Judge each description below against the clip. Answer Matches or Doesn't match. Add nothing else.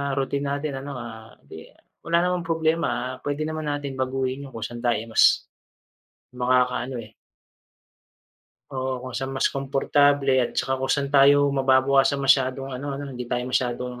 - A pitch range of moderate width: Doesn't match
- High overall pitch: Doesn't match